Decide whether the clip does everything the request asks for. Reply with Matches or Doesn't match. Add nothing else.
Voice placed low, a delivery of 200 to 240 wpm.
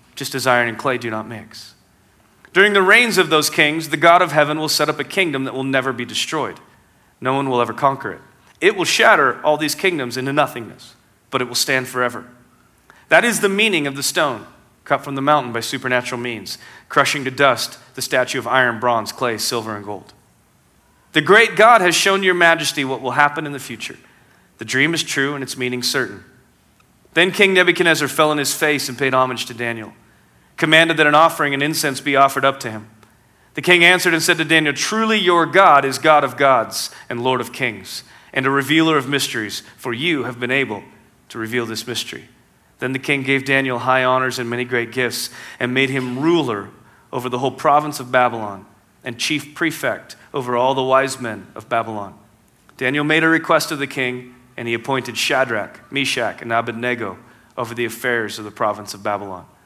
Matches